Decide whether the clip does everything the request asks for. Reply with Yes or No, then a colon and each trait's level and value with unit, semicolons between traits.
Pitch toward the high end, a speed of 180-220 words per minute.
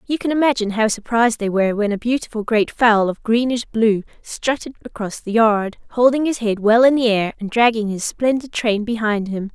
Yes: high, 225 Hz; fast, 205 wpm